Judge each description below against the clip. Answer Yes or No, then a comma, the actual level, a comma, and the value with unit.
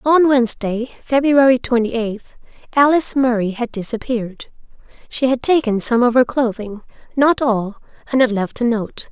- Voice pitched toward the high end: Yes, high, 240 Hz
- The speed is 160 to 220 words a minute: No, average, 145 wpm